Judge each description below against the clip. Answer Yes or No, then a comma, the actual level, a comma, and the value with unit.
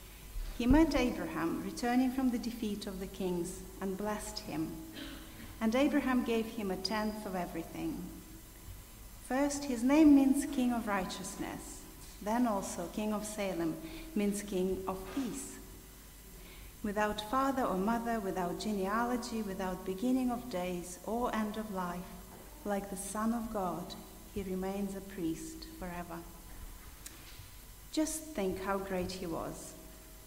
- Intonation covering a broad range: No, average, 4.4 semitones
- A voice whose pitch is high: Yes, high, 200 Hz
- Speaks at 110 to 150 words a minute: Yes, slow, 135 wpm